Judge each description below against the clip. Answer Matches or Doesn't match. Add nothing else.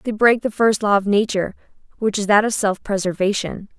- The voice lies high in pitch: Matches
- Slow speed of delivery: Doesn't match